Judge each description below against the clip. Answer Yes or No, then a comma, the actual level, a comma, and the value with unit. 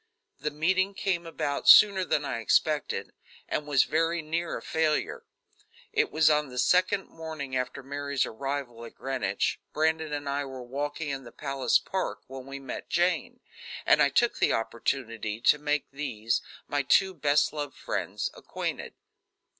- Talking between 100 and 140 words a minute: No, average, 160 wpm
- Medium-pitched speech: Yes, medium, 145 Hz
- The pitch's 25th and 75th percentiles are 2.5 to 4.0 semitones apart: Yes, average, 3.2 semitones